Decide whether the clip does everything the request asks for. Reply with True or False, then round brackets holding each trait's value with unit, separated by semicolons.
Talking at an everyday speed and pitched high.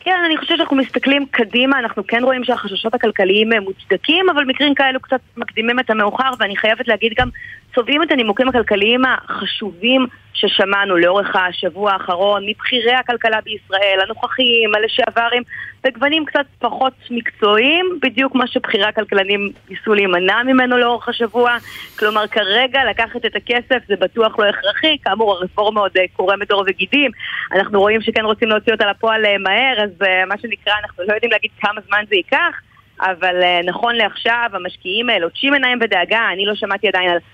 False (155 wpm; 225 Hz)